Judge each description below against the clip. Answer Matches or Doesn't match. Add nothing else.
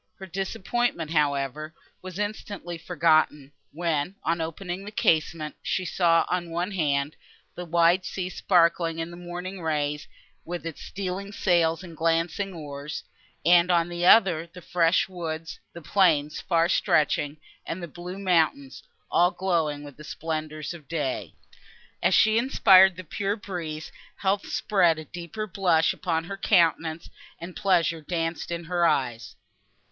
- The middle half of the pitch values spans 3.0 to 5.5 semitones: Doesn't match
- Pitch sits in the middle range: Matches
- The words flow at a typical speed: Matches